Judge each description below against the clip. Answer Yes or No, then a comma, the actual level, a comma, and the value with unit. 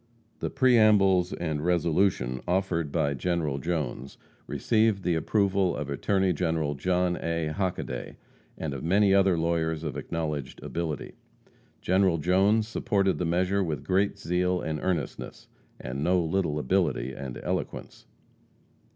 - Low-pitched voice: Yes, very low, 85 Hz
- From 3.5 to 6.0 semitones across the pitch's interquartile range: Yes, average, 3.8 semitones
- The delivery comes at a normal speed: No, slow, 130 wpm